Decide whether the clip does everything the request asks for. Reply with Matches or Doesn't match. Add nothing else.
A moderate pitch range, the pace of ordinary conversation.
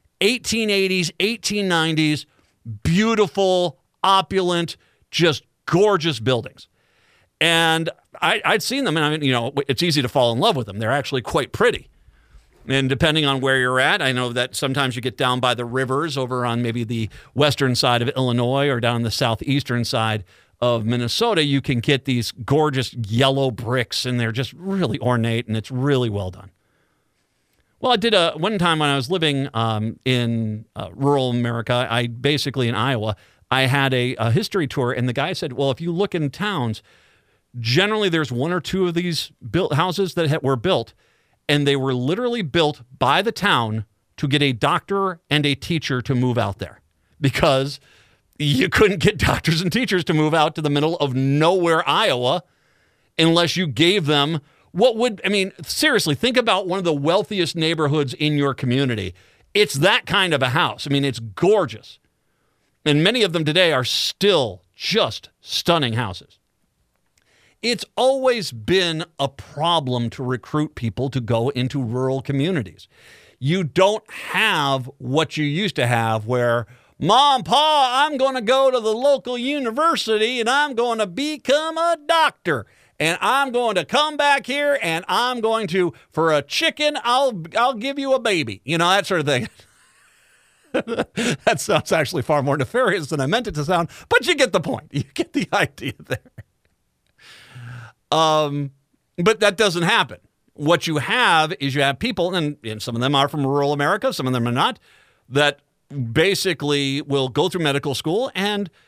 Doesn't match